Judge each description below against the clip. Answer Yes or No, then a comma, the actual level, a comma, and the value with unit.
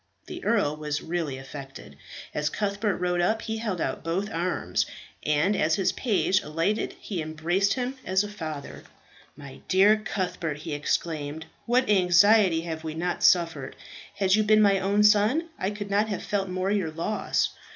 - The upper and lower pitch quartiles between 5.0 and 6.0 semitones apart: No, average, 4.5 semitones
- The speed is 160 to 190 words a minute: Yes, average, 170 wpm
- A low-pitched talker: No, medium, 185 Hz